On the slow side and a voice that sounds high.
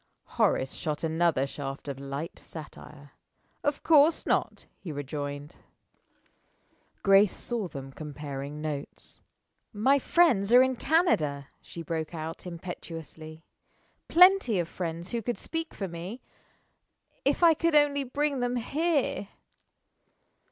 No: slow, 120 wpm; medium, 175 Hz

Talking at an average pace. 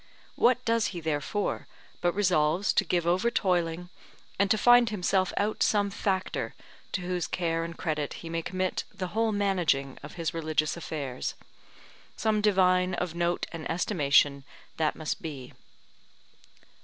Yes: average, 145 wpm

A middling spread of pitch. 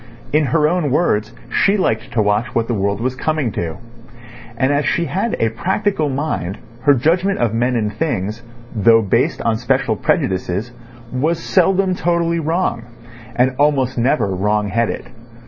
No: wide, 6.6 semitones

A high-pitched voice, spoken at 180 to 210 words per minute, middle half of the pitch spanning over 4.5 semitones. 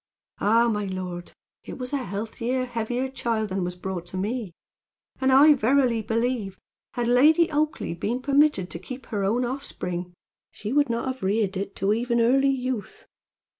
No: high, 230 Hz; average, 170 wpm; average, 4.9 semitones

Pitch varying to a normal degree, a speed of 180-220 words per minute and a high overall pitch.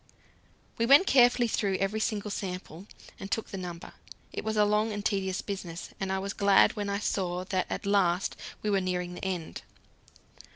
No: narrow, 2.3 semitones; average, 195 wpm; high, 195 Hz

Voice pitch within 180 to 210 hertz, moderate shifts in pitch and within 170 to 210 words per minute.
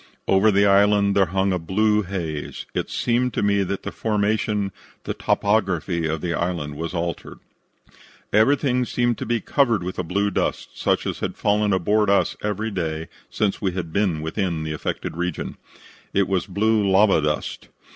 No: low, 100 Hz; average, 3.4 semitones; average, 175 wpm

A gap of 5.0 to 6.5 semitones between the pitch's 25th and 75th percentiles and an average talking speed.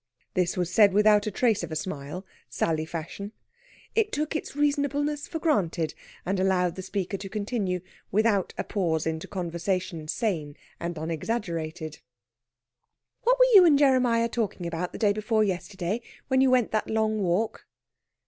Yes: average, 5.3 semitones; average, 160 wpm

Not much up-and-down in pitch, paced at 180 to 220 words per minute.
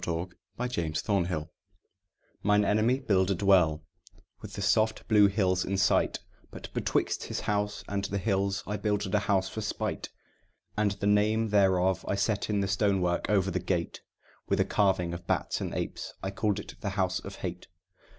Yes: narrow, 2.0 semitones; average, 185 wpm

